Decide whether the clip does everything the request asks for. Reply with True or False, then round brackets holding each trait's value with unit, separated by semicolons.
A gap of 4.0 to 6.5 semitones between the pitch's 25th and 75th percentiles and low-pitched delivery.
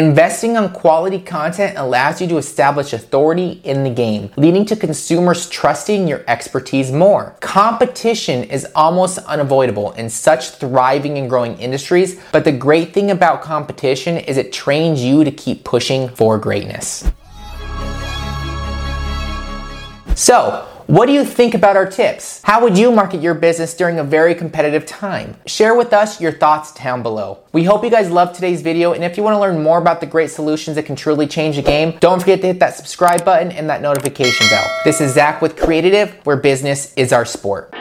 False (5.2 semitones; 155 Hz)